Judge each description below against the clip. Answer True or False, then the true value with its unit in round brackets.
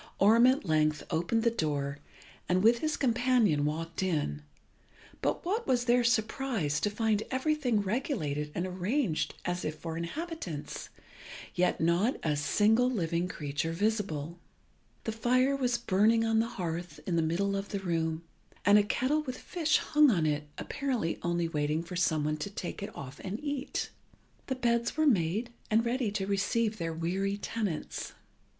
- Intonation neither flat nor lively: False (6.5 semitones)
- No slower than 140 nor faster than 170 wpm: True (165 wpm)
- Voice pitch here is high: True (200 Hz)